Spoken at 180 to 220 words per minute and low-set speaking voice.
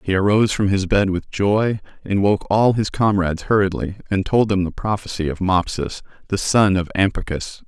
Yes: average, 195 wpm; low, 100 Hz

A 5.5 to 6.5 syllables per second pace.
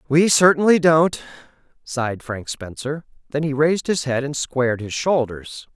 No: 4.7 syllables/s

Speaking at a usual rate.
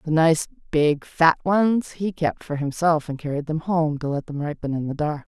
No: fast, 225 wpm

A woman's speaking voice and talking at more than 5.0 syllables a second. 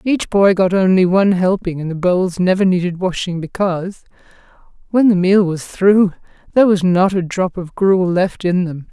No: female; 4.9 syllables/s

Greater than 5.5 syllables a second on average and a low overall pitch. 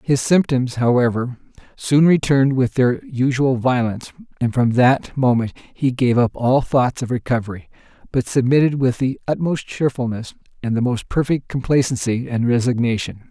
No: 4.9 syllables/s; low, 130 Hz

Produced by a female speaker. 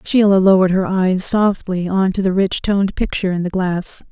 Yes: female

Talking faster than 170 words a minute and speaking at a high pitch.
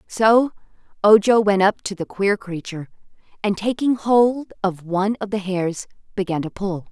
No: average, 165 wpm; high, 200 Hz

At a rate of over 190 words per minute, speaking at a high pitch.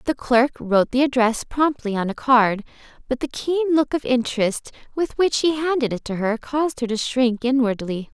Yes: average, 200 wpm; very high, 250 Hz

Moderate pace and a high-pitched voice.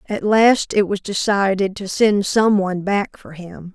Yes: average, 190 wpm; high, 200 Hz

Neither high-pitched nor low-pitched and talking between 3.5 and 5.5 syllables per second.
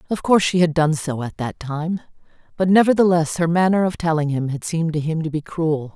No: medium, 165 Hz; 5.8 syllables/s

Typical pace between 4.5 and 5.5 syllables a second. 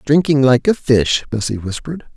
Yes: 5.2 syllables/s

